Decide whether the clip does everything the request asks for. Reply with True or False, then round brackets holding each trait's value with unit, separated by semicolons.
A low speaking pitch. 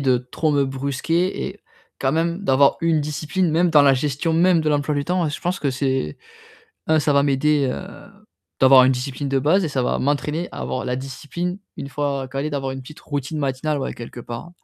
False (145 Hz)